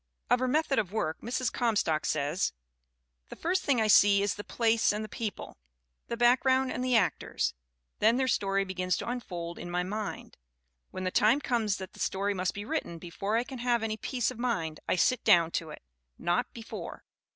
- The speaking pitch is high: Yes, high, 215 Hz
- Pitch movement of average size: Yes, average, 5.0 semitones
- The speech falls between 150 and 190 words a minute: No, fast, 205 wpm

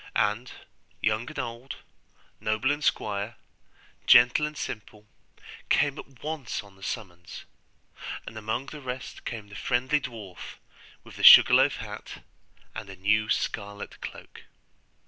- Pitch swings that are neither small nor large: Yes, average, 4.0 semitones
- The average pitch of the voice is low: Yes, low, 110 Hz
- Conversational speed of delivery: No, slow, 130 wpm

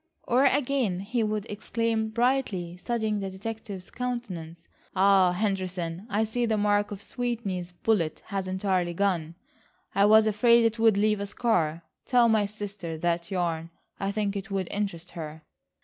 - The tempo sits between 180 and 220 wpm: No, average, 155 wpm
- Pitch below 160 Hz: No, high, 200 Hz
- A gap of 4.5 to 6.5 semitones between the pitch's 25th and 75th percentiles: No, average, 3.6 semitones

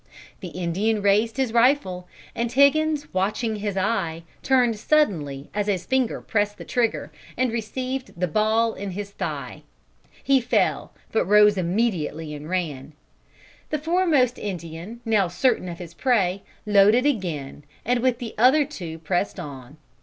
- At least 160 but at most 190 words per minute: No, average, 145 wpm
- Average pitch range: No, wide, 5.7 semitones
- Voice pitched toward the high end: Yes, high, 210 Hz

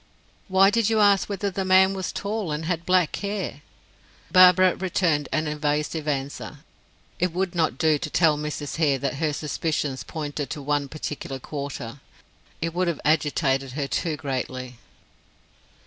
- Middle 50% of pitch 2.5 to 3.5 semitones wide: No, average, 4.1 semitones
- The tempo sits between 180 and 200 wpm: No, average, 155 wpm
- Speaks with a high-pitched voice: No, medium, 155 Hz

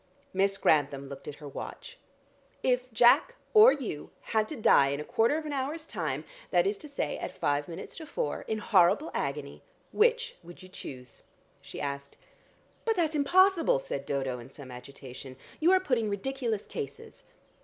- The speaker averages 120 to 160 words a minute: No, average, 175 wpm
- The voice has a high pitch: Yes, high, 200 Hz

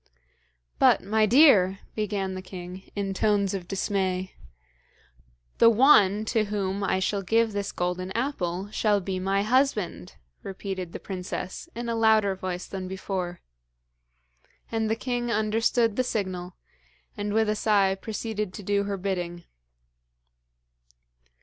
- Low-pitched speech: No, high, 200 Hz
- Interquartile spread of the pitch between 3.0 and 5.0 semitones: No, narrow, 2.6 semitones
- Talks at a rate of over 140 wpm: No, slow, 135 wpm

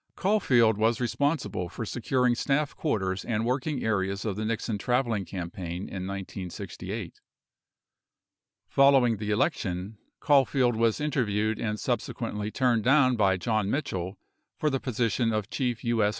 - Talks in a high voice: No, low, 115 Hz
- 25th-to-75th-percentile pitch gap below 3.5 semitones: No, average, 3.8 semitones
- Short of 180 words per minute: Yes, slow, 135 wpm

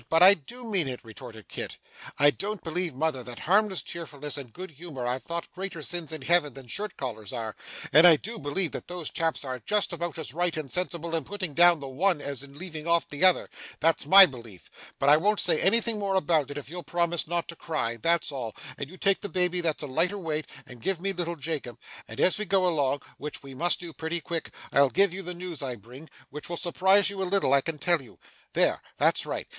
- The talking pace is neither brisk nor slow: No, fast, 235 wpm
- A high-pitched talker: No, medium, 165 Hz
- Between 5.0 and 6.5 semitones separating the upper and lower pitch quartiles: No, average, 4.3 semitones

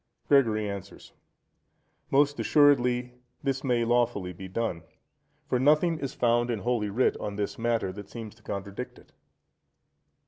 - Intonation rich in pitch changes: No, average, 3.7 semitones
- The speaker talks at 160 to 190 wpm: No, slow, 135 wpm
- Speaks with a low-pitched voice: Yes, low, 120 Hz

